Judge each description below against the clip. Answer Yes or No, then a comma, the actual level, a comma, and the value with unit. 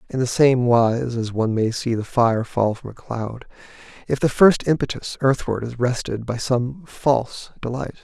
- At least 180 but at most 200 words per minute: Yes, average, 185 wpm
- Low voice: Yes, low, 120 Hz